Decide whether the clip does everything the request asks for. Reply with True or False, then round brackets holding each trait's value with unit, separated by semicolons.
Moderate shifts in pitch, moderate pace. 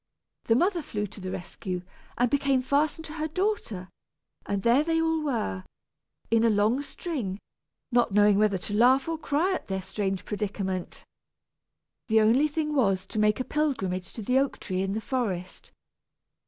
False (6.8 semitones; 170 wpm)